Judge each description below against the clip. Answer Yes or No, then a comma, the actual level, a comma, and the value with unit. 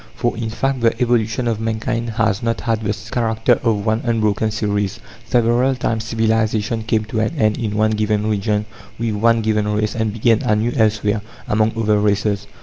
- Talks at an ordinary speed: Yes, average, 180 wpm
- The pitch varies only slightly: Yes, narrow, 1.4 semitones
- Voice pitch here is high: No, low, 110 Hz